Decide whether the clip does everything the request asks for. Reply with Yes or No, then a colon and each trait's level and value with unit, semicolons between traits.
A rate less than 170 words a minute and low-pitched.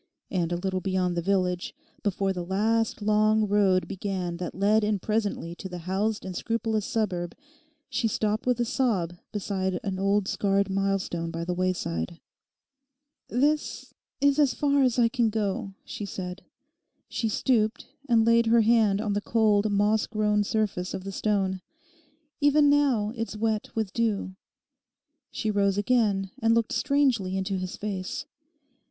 No: average, 155 wpm; high, 205 Hz